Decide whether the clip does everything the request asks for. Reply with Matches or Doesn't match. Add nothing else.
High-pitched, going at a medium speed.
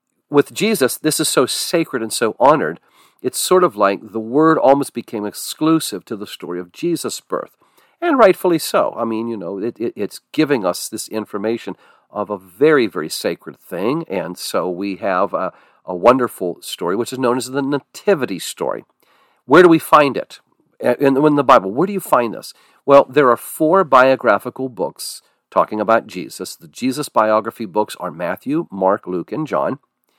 Doesn't match